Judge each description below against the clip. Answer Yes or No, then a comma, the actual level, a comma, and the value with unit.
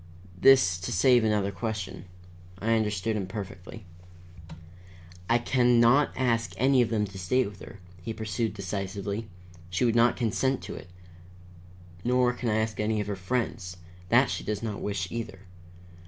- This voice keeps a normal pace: Yes, average, 160 wpm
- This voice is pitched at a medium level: No, low, 110 Hz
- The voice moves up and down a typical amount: Yes, average, 3.4 semitones